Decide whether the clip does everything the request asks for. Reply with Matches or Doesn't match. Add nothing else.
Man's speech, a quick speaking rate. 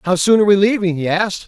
Matches